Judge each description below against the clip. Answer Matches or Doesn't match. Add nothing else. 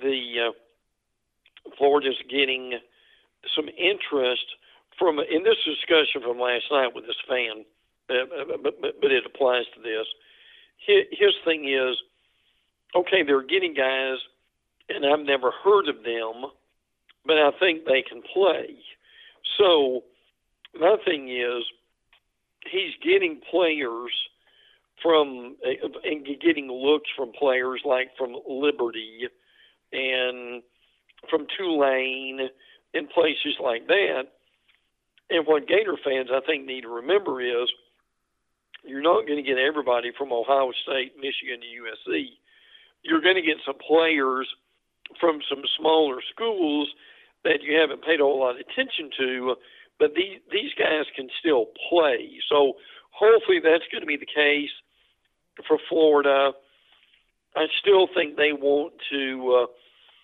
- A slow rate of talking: Matches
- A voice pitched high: Doesn't match